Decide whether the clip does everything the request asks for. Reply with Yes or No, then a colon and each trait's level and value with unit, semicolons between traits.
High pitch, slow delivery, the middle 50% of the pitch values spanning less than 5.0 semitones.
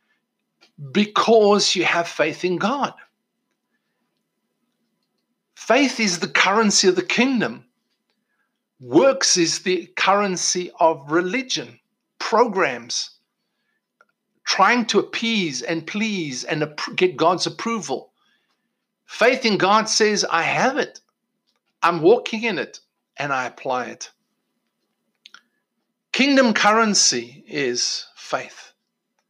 Yes: high, 205 Hz; slow, 100 wpm; average, 4.6 semitones